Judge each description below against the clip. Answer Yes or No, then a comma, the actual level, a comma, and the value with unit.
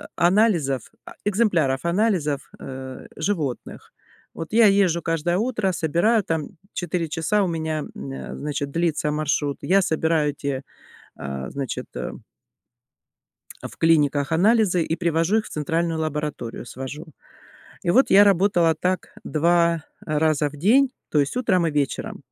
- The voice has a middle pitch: Yes, medium, 165 Hz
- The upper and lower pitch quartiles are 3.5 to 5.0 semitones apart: Yes, average, 3.8 semitones